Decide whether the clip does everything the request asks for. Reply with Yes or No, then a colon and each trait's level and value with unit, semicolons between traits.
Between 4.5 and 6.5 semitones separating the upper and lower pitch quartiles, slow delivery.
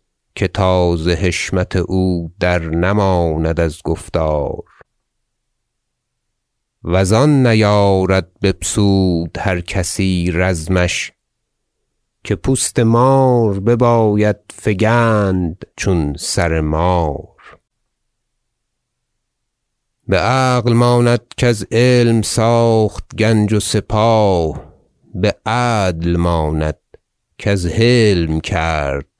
Yes: average, 5.1 semitones; slow, 80 wpm